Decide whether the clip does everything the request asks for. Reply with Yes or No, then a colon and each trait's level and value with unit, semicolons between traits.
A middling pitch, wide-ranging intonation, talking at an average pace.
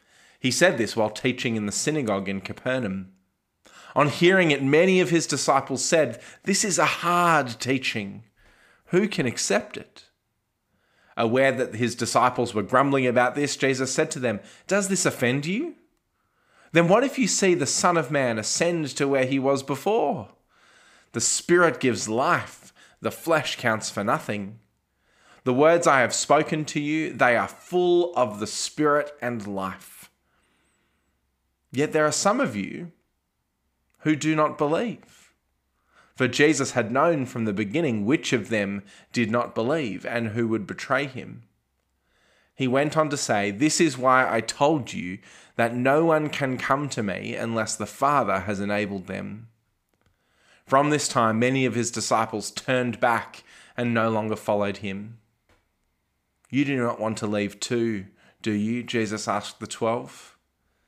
No: low, 125 Hz; wide, 5.8 semitones; average, 160 wpm